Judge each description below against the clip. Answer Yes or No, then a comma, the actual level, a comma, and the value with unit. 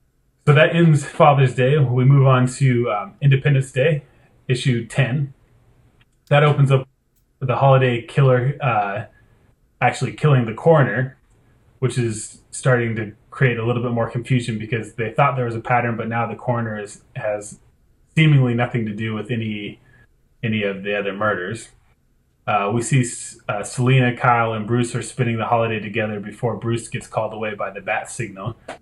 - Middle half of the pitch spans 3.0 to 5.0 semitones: No, narrow, 2.5 semitones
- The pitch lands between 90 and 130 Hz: Yes, low, 120 Hz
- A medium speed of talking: Yes, average, 170 wpm